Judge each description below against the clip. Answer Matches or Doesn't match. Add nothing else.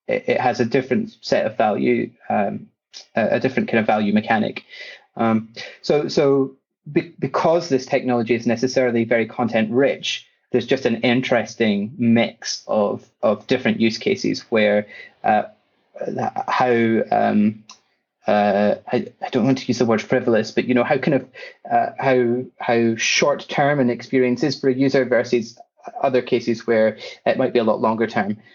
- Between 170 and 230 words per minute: Doesn't match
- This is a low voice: Matches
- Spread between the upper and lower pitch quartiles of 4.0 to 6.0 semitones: Doesn't match